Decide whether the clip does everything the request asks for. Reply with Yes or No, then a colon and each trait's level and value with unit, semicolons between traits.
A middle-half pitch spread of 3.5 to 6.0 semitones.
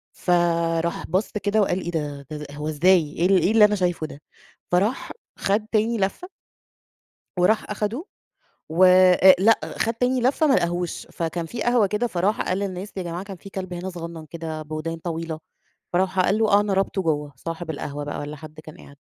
Yes: average, 3.9 semitones